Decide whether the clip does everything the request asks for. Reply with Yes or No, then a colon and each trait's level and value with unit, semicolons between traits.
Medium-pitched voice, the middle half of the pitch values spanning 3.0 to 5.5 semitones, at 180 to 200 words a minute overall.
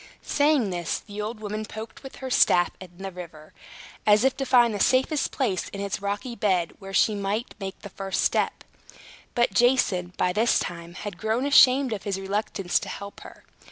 No: high, 205 Hz; average, 3.9 semitones; average, 190 wpm